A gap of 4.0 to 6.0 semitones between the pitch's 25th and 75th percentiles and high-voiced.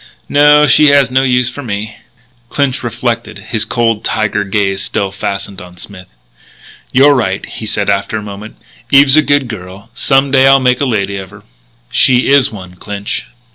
No: average, 5.1 semitones; low, 110 Hz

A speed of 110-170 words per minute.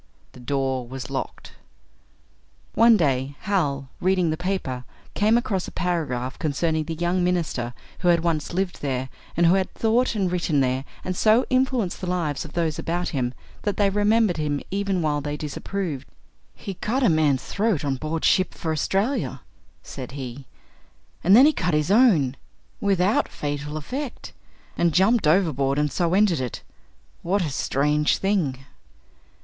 Yes: average, 160 wpm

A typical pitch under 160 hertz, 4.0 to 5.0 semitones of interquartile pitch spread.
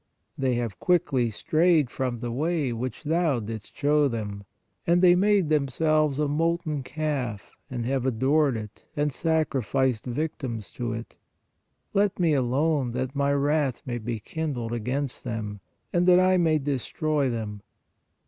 Yes: low, 135 Hz; average, 4.6 semitones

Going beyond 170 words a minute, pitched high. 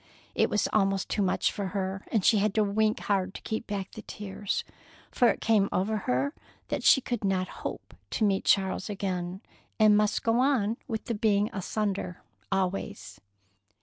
Yes: average, 180 wpm; high, 200 Hz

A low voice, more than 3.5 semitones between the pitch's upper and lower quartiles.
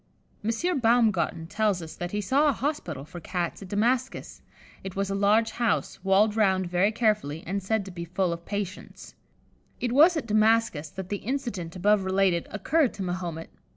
No: high, 200 Hz; average, 4.1 semitones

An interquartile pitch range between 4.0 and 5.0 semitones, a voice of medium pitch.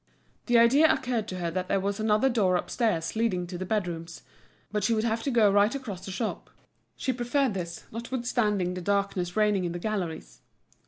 No: average, 4.3 semitones; high, 210 Hz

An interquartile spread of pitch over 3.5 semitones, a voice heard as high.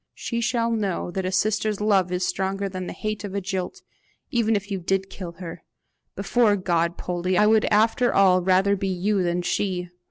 No: narrow, 2.6 semitones; high, 195 Hz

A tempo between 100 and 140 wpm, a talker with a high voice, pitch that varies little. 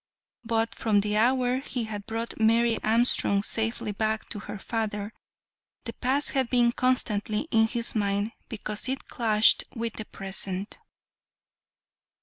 Yes: slow, 135 wpm; high, 225 Hz; narrow, 2.1 semitones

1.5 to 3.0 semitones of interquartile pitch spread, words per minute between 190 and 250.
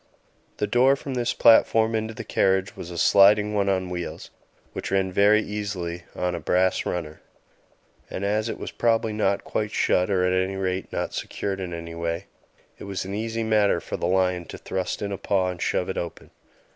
Yes: average, 2.7 semitones; average, 200 wpm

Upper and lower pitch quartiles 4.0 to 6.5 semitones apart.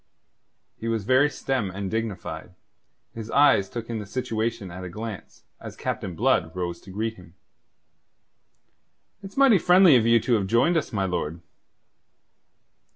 Yes: average, 5.2 semitones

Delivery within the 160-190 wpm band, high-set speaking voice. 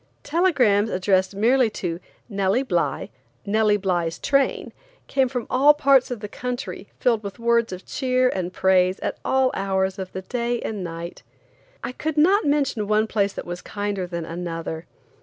Yes: average, 165 wpm; high, 210 Hz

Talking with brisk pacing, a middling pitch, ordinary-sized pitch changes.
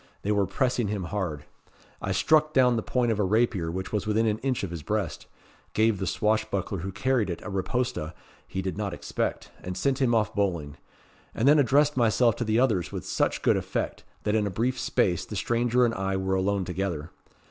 No: fast, 210 wpm; low, 105 Hz; average, 4.1 semitones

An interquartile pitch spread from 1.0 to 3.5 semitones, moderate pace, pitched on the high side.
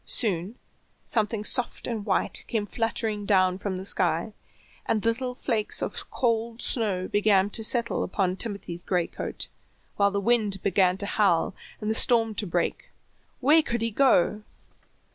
Yes: average, 3.1 semitones; average, 155 wpm; high, 210 Hz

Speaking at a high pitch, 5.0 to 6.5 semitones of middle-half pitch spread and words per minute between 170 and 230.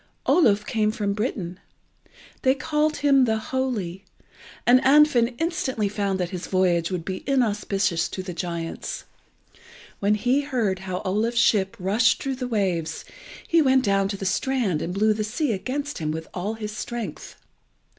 No: high, 210 Hz; average, 5.3 semitones; average, 160 wpm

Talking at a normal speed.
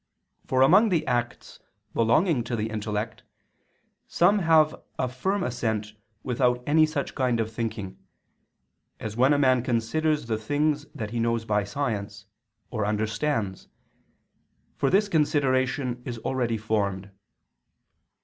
No: slow, 130 wpm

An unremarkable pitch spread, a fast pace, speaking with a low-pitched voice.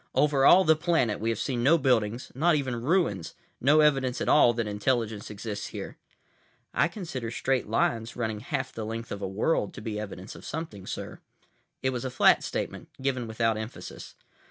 No: average, 4.2 semitones; average, 185 wpm; low, 120 Hz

